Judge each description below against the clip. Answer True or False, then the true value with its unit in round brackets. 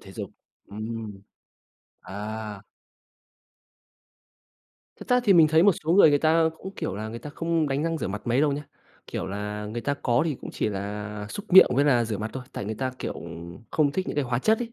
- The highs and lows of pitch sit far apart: True (7.1 semitones)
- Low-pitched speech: True (130 Hz)